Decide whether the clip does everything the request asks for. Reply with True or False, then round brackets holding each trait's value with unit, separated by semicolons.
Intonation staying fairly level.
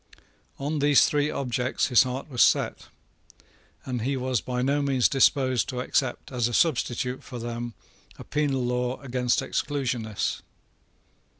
True (2.1 semitones)